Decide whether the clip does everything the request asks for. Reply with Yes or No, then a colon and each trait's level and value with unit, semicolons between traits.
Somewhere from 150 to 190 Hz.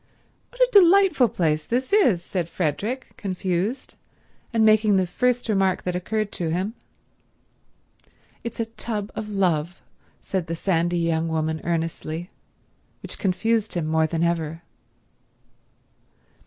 Yes: medium, 185 Hz